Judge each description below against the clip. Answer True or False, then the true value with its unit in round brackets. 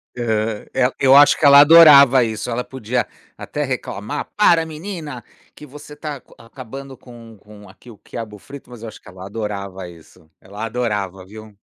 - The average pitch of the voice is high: False (120 Hz)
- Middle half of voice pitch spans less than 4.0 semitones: False (5.0 semitones)